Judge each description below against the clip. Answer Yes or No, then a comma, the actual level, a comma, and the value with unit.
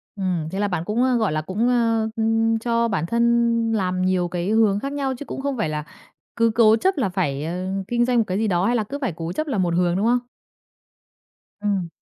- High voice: Yes, high, 215 Hz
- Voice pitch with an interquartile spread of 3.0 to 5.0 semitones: Yes, average, 4.5 semitones